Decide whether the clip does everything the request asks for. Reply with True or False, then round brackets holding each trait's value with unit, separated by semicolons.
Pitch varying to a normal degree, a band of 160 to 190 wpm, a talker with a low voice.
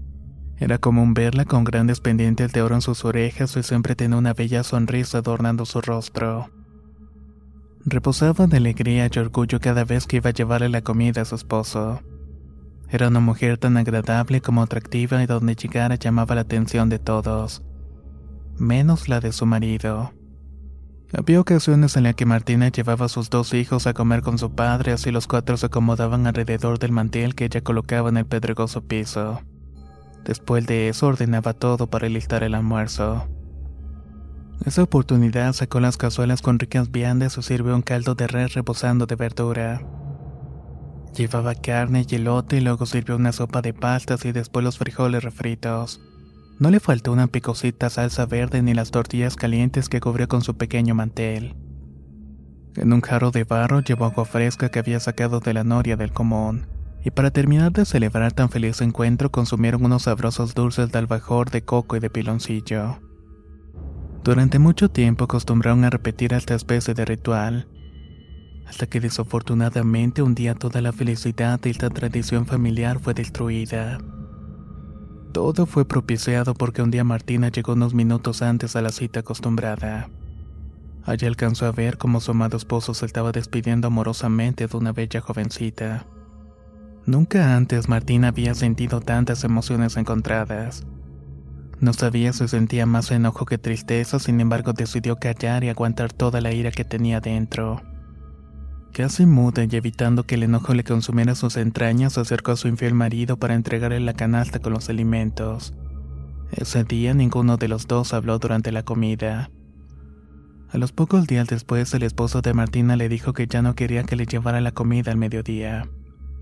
False (1.5 semitones; 165 wpm; 120 Hz)